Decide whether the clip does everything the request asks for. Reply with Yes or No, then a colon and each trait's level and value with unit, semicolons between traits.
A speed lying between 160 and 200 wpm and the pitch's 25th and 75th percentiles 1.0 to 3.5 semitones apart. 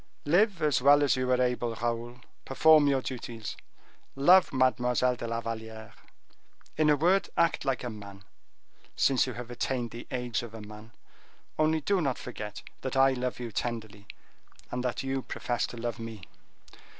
Yes: average, 170 wpm; average, 2.9 semitones